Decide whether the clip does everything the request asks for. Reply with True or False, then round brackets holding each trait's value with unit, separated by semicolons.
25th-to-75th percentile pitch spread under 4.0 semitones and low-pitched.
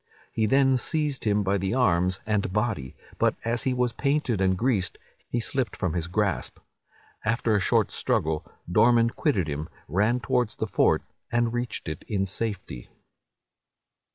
False (4.5 semitones; 110 Hz)